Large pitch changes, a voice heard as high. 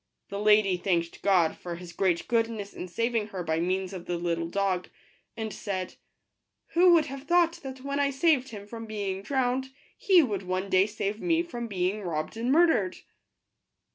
Yes: wide, 6.1 semitones; high, 205 Hz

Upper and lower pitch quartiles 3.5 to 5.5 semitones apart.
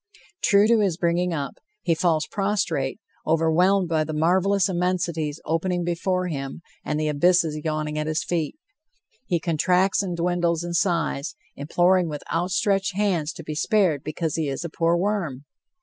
No: average, 2.9 semitones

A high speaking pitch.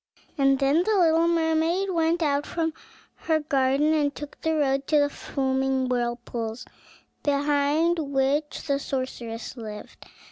Yes: very high, 285 Hz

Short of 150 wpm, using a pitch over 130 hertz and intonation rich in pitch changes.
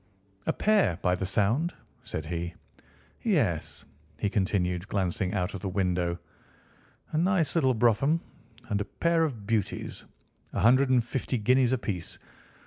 No: average, 140 wpm; low, 105 Hz; wide, 6.3 semitones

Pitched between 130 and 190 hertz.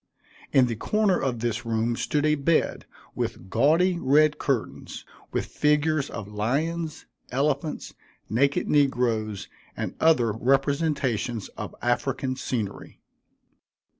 Yes: low, 135 Hz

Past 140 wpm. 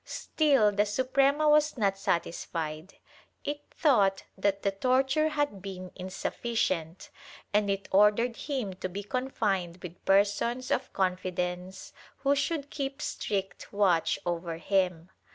No: slow, 135 wpm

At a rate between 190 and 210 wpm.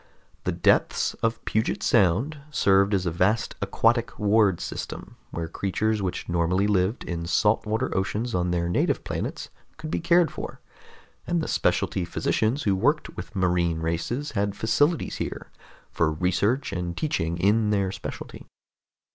No: average, 150 wpm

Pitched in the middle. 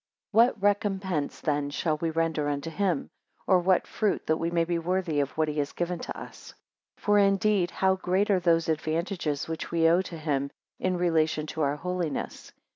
Yes: medium, 170 Hz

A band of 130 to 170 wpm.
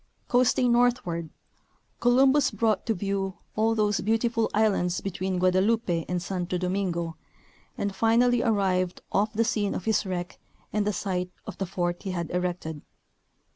Yes: average, 145 wpm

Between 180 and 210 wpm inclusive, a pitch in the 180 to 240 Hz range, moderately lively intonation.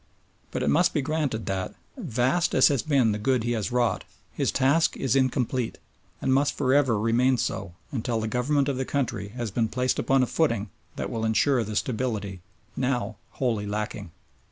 No: average, 185 wpm; low, 125 Hz; average, 3.5 semitones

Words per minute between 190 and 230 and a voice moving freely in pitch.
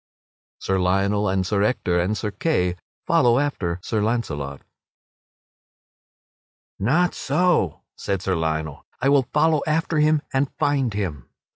No: slow, 135 wpm; wide, 7.9 semitones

